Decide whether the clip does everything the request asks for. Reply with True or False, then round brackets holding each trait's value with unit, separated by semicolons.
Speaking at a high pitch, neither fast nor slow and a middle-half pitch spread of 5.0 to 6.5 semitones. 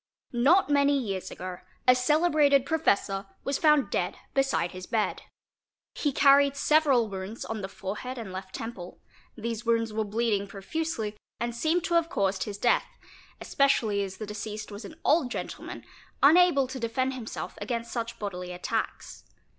True (235 Hz; 160 wpm; 5.5 semitones)